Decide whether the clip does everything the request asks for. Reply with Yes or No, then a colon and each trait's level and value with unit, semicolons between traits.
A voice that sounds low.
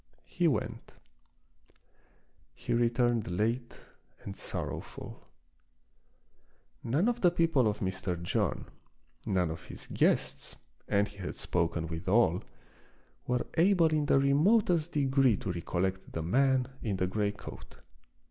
Yes: low, 115 Hz